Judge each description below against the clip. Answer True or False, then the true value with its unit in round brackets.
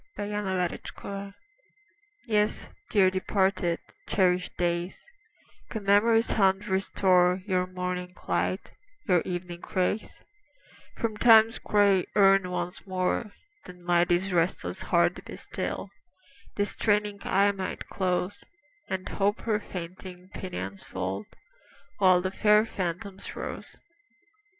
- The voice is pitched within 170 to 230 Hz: True (190 Hz)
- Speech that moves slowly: True (110 wpm)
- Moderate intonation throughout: False (2.2 semitones)